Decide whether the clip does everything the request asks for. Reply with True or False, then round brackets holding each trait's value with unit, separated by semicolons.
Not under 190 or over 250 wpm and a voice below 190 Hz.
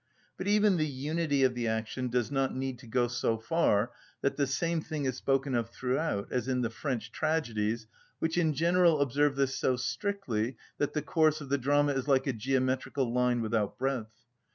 True (195 wpm; 135 Hz)